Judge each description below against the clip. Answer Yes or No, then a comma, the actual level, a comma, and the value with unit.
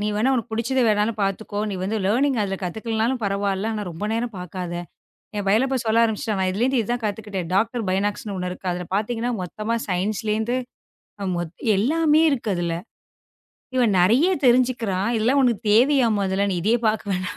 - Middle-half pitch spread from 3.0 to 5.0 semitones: Yes, average, 3.6 semitones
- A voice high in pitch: Yes, high, 215 Hz